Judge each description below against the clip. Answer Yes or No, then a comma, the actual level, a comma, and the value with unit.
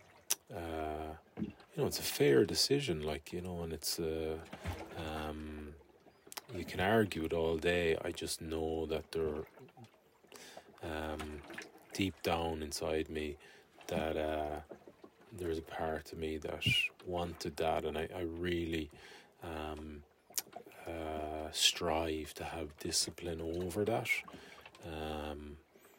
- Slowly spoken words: Yes, slow, 125 wpm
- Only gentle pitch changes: Yes, narrow, 1.5 semitones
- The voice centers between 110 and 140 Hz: No, very low, 80 Hz